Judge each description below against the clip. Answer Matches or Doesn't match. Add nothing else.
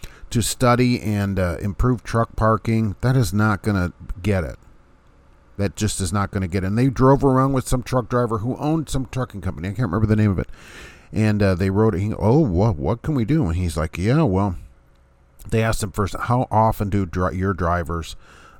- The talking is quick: Matches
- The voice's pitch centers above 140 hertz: Doesn't match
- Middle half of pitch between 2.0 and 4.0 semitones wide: Doesn't match